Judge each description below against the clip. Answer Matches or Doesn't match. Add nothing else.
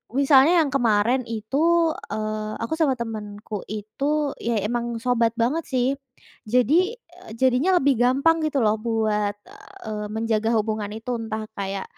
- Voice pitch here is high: Matches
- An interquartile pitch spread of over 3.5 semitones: Matches